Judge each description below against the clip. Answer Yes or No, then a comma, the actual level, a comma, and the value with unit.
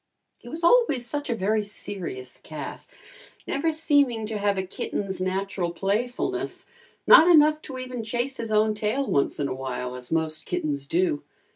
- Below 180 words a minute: Yes, average, 165 wpm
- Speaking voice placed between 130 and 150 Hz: No, high, 210 Hz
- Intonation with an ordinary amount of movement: No, wide, 6.8 semitones